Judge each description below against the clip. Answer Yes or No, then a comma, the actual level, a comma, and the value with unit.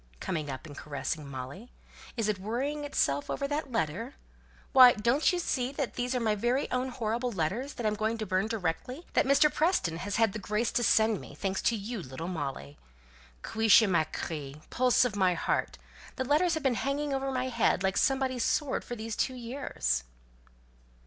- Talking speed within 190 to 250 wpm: Yes, average, 195 wpm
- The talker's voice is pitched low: No, high, 225 Hz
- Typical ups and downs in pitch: No, wide, 6.0 semitones